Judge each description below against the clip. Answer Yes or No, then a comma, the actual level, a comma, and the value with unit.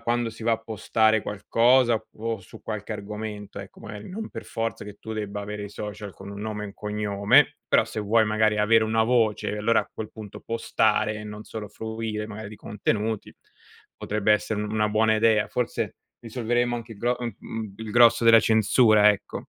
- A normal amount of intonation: No, narrow, 1.4 semitones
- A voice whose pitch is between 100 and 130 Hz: Yes, low, 110 Hz